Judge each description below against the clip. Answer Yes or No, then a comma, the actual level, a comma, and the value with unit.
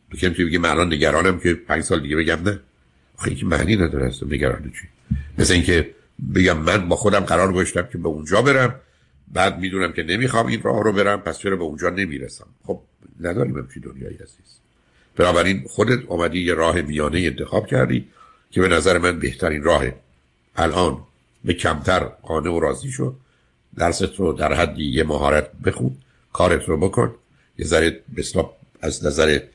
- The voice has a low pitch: Yes, very low, 85 Hz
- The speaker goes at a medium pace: No, fast, 165 wpm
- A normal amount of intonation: Yes, average, 4.9 semitones